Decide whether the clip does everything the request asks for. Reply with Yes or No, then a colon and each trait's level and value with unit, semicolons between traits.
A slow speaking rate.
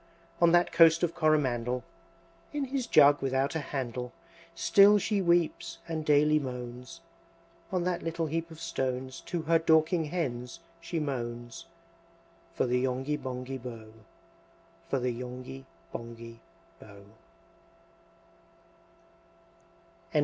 Yes: slow, 115 wpm